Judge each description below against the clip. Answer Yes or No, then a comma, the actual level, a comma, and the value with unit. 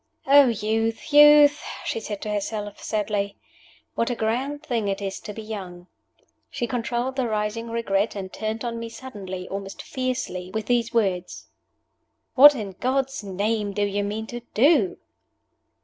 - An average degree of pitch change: Yes, average, 3.4 semitones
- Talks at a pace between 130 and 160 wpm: Yes, average, 155 wpm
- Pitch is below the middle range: No, high, 220 Hz